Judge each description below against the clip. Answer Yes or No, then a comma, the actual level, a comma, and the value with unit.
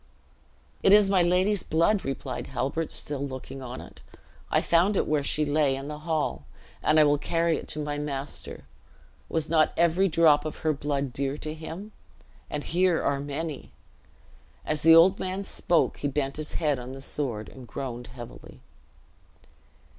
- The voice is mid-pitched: Yes, medium, 150 Hz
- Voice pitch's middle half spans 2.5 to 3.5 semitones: Yes, average, 3.2 semitones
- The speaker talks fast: No, average, 170 wpm